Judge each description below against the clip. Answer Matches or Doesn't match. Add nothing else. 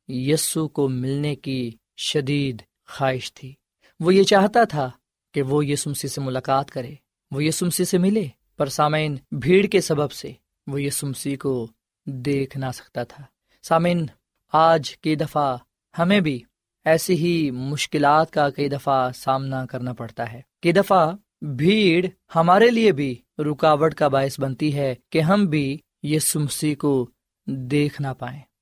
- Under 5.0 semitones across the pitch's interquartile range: Matches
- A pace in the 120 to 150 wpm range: Matches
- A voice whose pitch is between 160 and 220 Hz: Doesn't match